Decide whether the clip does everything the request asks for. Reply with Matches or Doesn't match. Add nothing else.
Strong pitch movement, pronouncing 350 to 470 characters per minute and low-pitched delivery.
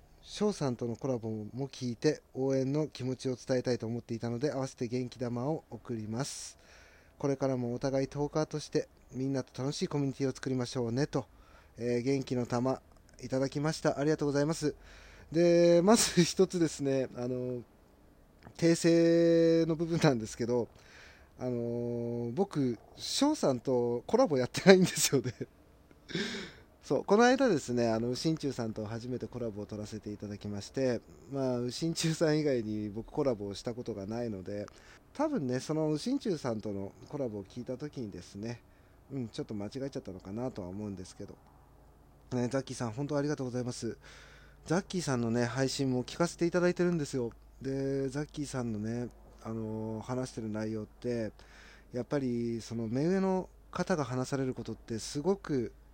Doesn't match